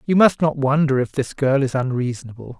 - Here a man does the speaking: Yes, male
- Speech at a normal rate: No, fast, 210 wpm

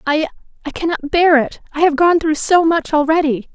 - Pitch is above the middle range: Yes, very high, 310 Hz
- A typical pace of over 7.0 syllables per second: No, 5.4 syllables/s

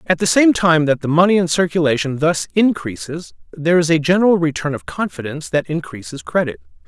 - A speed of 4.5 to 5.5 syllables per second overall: No, 5.9 syllables/s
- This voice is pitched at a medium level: Yes, medium, 160 Hz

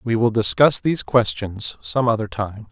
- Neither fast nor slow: Yes, average, 175 wpm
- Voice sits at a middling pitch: No, low, 115 Hz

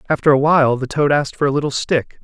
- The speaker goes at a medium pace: No, fast, 270 wpm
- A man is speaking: Yes, male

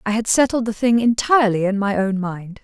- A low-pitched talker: No, high, 215 Hz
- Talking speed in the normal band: No, fast, 230 wpm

